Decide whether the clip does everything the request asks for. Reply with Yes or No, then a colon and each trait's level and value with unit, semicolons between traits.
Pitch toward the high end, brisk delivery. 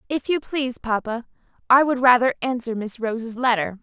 No: high, 245 Hz; average, 175 wpm